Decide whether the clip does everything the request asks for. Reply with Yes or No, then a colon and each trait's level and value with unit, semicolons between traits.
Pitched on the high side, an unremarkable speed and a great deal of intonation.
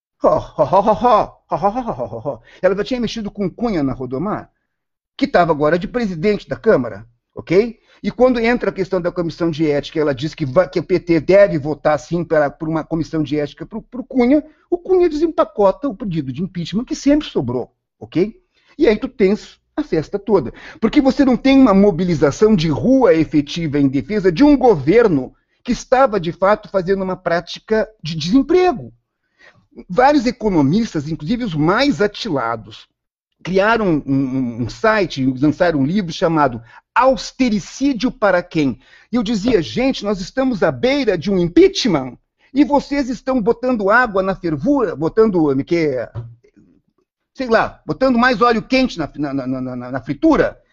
Yes: high, 195 Hz; average, 155 wpm; wide, 8.1 semitones